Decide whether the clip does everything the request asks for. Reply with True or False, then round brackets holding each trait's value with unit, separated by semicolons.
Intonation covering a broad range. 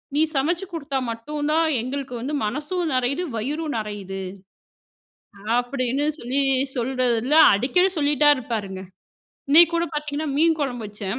False (4.2 semitones)